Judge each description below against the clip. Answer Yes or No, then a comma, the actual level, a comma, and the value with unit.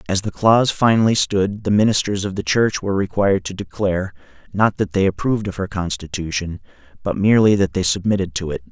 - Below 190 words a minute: No, average, 195 wpm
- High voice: No, low, 100 Hz